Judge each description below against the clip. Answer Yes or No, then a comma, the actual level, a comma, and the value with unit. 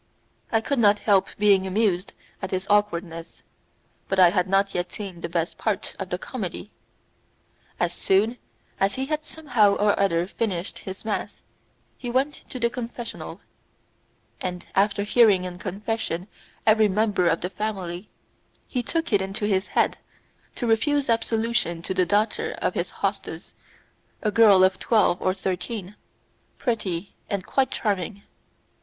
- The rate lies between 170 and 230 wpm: No, average, 150 wpm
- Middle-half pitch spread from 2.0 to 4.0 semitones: Yes, average, 3.4 semitones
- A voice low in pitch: No, high, 205 Hz